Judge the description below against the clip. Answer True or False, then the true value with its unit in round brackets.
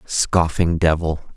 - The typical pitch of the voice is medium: False (80 Hz)